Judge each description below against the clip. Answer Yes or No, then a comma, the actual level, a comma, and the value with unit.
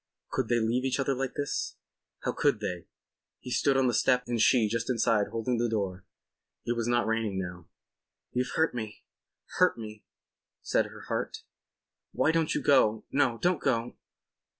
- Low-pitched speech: Yes, low, 120 Hz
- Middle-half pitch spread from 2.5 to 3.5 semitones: Yes, average, 2.9 semitones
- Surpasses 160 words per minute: Yes, average, 170 wpm